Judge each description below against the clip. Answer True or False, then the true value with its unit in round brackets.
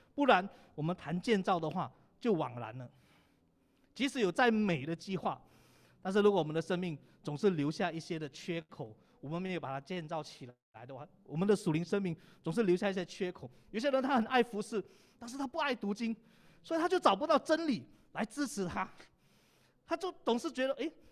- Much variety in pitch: True (6.5 semitones)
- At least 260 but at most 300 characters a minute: True (290 characters per minute)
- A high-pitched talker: True (195 Hz)